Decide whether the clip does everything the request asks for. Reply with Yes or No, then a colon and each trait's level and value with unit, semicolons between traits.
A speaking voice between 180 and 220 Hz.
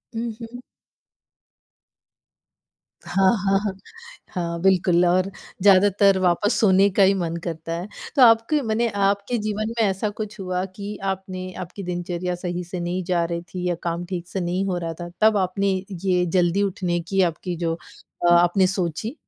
Yes: medium, 185 Hz